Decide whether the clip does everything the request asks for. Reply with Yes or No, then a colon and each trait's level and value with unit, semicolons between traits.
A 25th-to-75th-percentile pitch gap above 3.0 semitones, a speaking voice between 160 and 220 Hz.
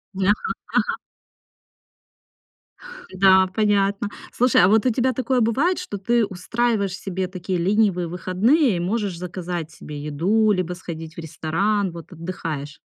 Yes: average, 3.7 semitones; high, 190 Hz